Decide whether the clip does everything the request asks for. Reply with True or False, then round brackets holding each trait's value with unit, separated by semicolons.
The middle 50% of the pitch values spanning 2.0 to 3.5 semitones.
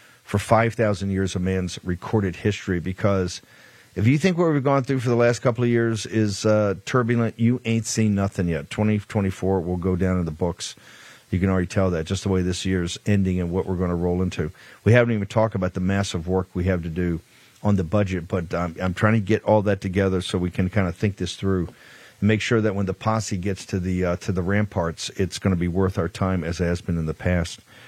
True (3.1 semitones)